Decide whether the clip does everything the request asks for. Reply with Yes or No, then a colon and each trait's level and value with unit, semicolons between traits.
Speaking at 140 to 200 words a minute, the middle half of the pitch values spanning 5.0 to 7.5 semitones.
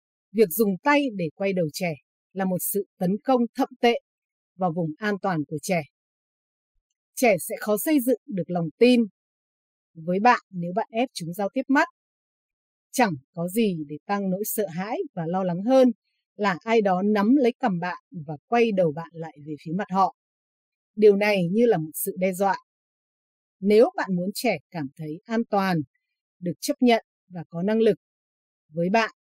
Yes: average, 185 wpm; average, 5.3 semitones